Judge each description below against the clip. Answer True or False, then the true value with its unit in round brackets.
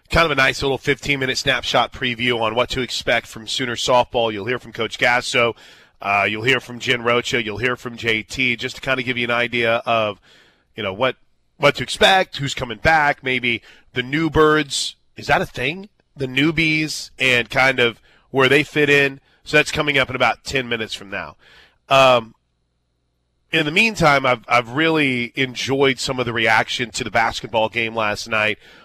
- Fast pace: False (195 wpm)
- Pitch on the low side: True (125 Hz)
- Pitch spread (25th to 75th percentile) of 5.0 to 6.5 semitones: False (3.3 semitones)